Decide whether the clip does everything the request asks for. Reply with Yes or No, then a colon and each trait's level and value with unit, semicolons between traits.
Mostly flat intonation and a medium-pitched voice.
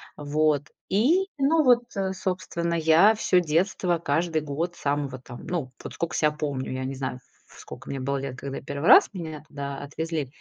No: average, 4.3 semitones; medium, 155 Hz